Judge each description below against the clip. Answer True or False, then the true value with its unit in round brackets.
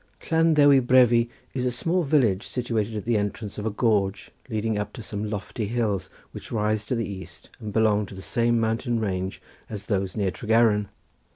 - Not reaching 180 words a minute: False (190 wpm)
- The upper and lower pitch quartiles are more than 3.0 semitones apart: False (2.7 semitones)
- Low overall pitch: True (110 Hz)